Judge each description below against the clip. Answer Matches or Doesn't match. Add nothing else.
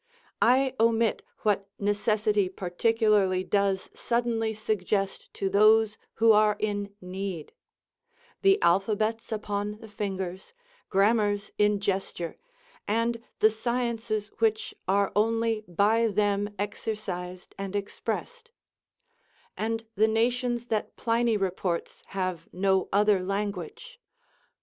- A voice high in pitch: Matches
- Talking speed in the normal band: Doesn't match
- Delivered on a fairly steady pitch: Matches